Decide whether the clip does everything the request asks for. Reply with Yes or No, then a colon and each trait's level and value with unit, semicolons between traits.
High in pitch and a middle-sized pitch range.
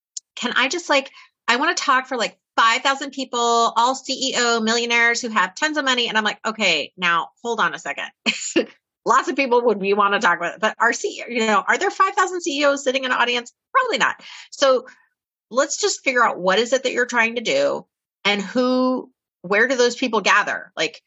Yes: very high, 250 Hz; average, 3.6 semitones